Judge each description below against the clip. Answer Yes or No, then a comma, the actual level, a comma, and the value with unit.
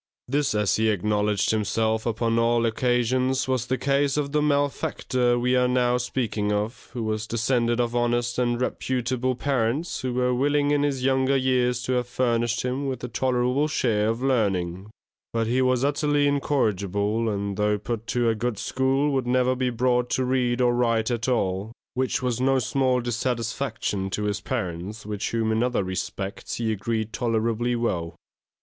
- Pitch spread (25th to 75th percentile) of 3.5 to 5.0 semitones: No, average, 2.7 semitones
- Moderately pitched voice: No, low, 120 Hz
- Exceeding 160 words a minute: Yes, average, 175 wpm